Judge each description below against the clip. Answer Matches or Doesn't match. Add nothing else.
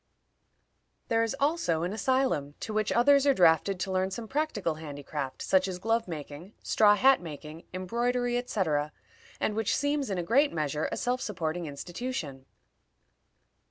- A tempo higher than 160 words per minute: Doesn't match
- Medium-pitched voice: Doesn't match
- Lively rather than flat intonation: Matches